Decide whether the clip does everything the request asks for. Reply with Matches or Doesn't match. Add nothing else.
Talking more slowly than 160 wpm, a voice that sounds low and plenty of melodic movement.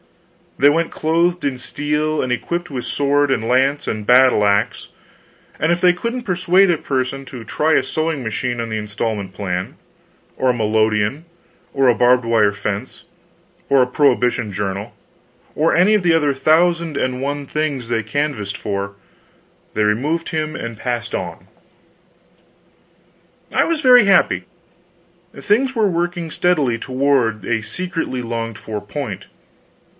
Matches